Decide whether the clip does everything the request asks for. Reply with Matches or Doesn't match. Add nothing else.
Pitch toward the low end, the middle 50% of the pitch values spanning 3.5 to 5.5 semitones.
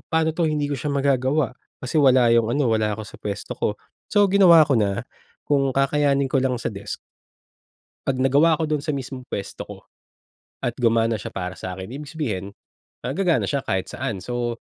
Matches